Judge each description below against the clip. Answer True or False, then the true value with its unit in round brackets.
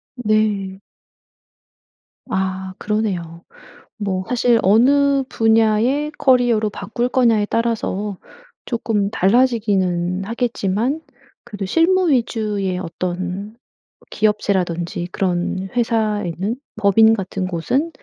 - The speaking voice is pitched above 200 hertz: True (210 Hz)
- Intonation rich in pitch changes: False (3.8 semitones)